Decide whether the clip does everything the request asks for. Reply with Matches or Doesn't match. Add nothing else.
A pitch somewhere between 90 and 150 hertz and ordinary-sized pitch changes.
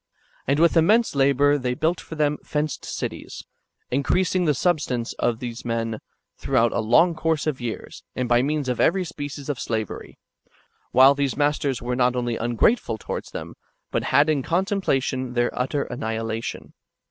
Matches